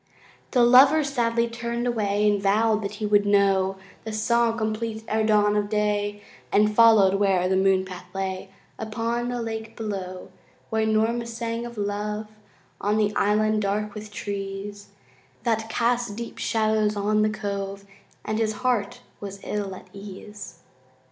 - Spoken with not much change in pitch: Yes, narrow, 2.0 semitones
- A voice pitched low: No, high, 210 Hz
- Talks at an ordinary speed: Yes, average, 150 wpm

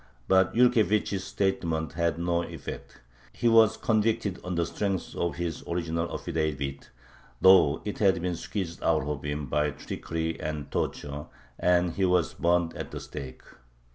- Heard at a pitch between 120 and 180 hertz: No, very low, 85 Hz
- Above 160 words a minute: No, average, 150 wpm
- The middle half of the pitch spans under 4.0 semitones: Yes, average, 3.3 semitones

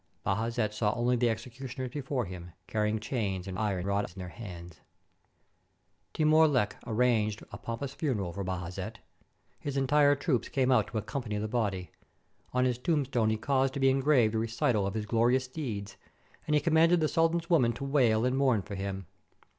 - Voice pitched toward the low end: Yes, low, 120 Hz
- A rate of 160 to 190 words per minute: Yes, average, 180 wpm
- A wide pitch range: No, average, 4.6 semitones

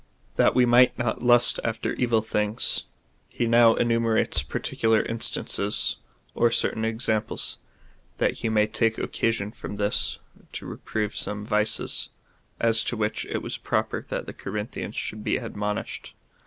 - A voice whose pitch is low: Yes, low, 110 Hz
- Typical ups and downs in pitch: No, narrow, 1.6 semitones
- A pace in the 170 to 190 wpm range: No, average, 145 wpm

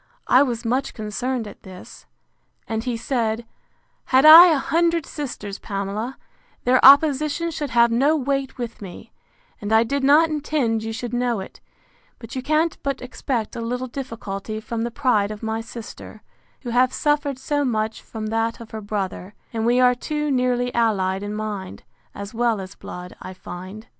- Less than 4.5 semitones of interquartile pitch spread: Yes, average, 3.9 semitones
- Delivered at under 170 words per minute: No, average, 175 wpm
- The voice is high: Yes, high, 235 Hz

